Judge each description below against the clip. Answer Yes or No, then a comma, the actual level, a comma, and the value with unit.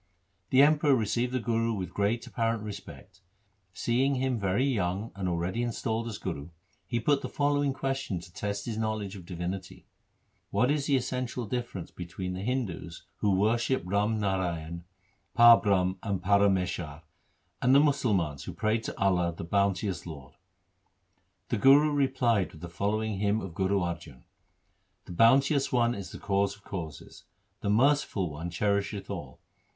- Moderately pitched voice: No, low, 100 Hz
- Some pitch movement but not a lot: Yes, average, 4.8 semitones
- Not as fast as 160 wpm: No, average, 165 wpm